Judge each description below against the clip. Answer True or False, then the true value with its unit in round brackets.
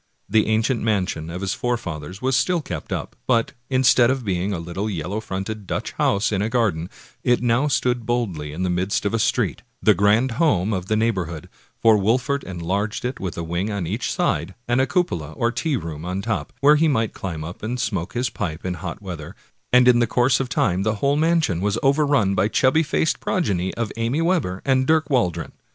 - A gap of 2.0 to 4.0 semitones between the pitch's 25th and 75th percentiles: False (5.5 semitones)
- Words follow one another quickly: True (210 wpm)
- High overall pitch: False (110 Hz)